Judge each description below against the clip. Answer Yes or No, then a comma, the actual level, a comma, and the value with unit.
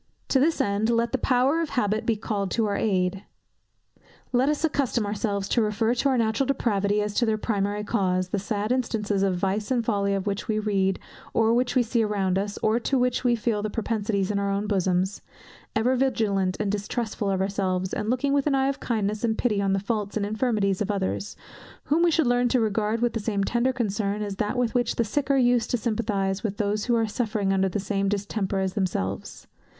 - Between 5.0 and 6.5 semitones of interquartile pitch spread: No, average, 3.2 semitones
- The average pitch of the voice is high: Yes, high, 210 Hz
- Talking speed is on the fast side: Yes, fast, 225 wpm